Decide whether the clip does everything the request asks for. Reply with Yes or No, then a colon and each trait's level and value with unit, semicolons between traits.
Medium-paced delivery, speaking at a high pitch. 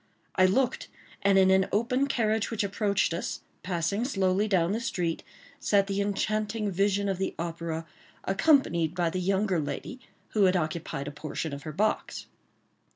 Yes: average, 160 wpm; high, 195 Hz